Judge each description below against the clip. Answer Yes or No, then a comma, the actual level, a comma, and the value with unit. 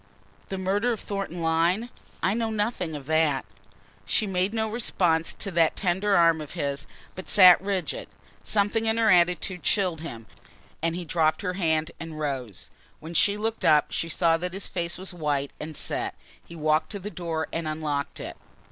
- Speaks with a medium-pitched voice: Yes, medium, 175 Hz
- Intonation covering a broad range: No, average, 3.9 semitones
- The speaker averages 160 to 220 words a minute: Yes, average, 185 wpm